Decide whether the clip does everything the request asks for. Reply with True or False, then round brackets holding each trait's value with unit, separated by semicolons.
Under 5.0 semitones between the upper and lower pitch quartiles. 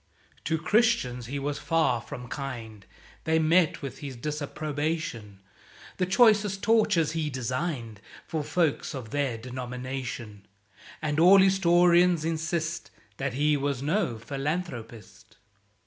False (5.3 semitones)